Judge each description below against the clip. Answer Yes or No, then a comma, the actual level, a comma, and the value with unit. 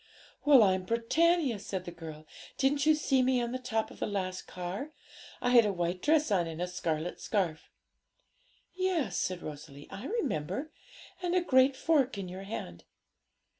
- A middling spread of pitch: No, wide, 7.6 semitones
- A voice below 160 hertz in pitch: No, high, 215 Hz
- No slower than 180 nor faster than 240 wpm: No, average, 170 wpm